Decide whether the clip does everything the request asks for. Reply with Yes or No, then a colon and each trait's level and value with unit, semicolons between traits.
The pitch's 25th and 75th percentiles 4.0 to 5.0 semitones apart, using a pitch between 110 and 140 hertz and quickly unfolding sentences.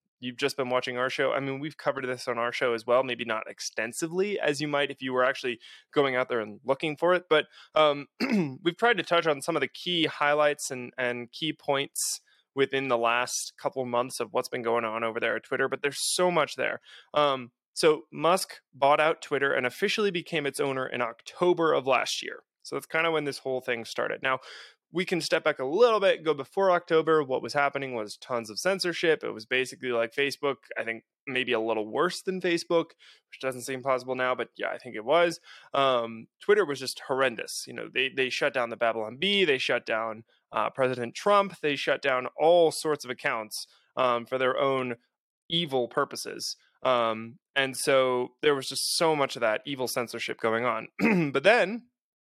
Yes: average, 4.3 semitones; low, 135 Hz; fast, 210 wpm